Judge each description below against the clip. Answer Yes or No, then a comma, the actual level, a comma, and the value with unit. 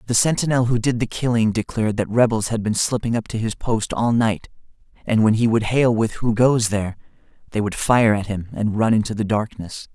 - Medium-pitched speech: No, low, 110 Hz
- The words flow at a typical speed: No, fast, 225 wpm